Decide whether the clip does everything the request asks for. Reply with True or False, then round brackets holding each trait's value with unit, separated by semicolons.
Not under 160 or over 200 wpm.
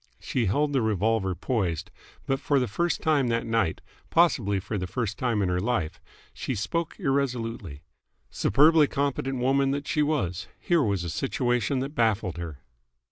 True (165 wpm)